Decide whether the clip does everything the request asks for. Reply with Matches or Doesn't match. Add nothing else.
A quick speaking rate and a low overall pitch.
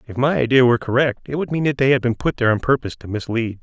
Matches